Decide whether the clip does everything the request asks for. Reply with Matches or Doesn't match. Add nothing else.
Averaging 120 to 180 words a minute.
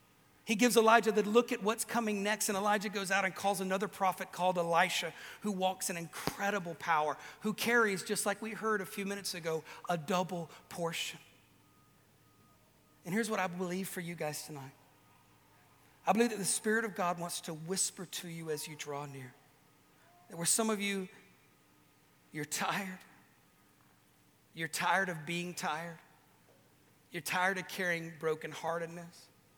Matches